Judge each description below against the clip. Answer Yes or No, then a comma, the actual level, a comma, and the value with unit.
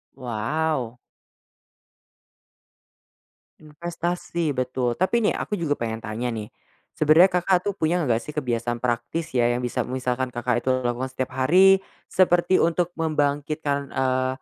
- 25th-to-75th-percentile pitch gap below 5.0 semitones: No, wide, 5.4 semitones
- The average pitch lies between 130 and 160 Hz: Yes, low, 135 Hz